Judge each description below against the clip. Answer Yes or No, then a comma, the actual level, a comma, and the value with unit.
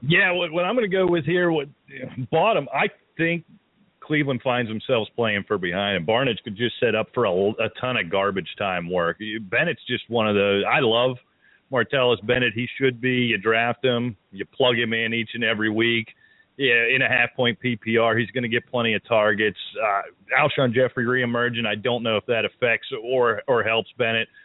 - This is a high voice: No, low, 120 Hz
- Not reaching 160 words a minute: No, fast, 205 wpm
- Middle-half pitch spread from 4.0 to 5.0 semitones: No, average, 2.8 semitones